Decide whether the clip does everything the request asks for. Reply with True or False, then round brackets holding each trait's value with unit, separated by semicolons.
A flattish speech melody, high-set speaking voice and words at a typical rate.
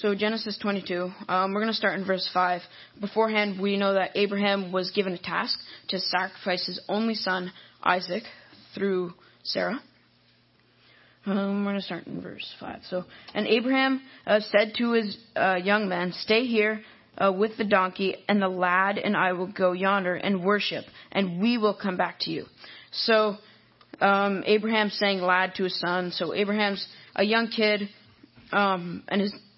True (2.2 semitones; 200 Hz; 170 wpm)